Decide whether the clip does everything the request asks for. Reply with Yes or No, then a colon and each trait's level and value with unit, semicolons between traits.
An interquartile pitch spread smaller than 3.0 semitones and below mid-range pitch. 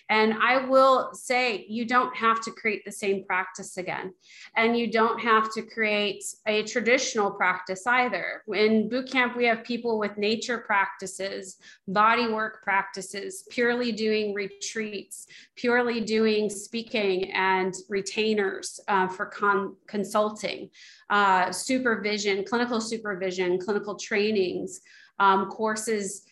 No: narrow, 2.6 semitones; high, 210 Hz